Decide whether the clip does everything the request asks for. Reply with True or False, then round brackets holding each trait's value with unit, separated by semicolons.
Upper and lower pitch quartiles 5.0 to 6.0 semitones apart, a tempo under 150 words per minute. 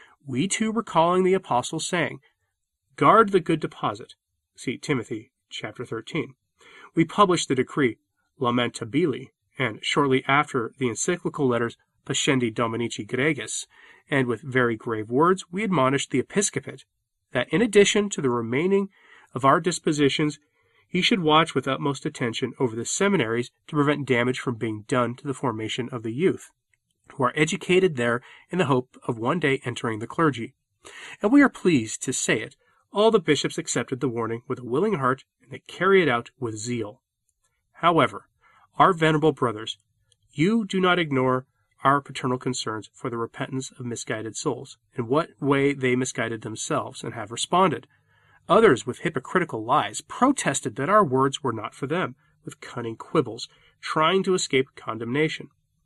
False (5.4 semitones; 160 wpm)